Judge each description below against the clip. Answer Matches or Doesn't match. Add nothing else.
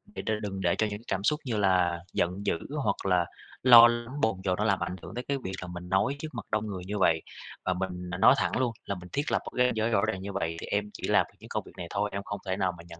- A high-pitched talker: Doesn't match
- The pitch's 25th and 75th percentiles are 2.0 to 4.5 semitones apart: Matches